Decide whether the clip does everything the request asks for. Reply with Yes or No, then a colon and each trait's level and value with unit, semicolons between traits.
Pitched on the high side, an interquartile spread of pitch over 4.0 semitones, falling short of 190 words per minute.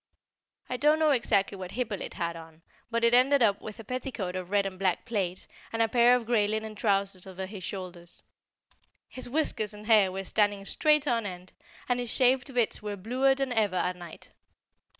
No: high, 210 Hz; average, 4.5 semitones; average, 195 wpm